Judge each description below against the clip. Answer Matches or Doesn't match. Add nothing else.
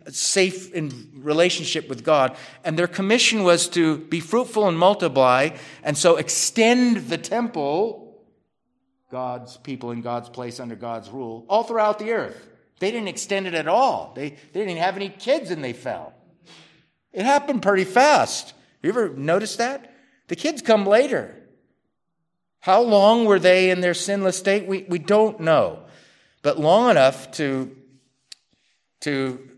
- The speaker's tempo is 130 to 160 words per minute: Matches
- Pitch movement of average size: Doesn't match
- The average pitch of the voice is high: Doesn't match